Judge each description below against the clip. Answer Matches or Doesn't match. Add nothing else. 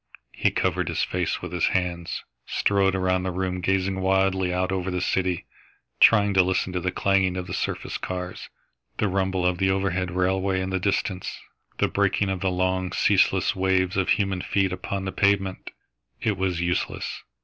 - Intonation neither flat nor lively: Doesn't match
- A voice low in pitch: Matches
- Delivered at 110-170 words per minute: Doesn't match